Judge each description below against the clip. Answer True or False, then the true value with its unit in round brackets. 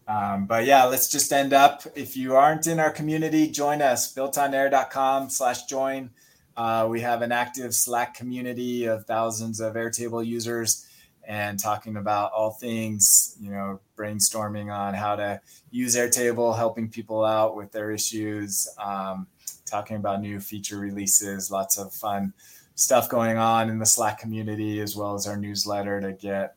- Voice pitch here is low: True (110 Hz)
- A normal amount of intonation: True (3.1 semitones)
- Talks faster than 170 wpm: False (165 wpm)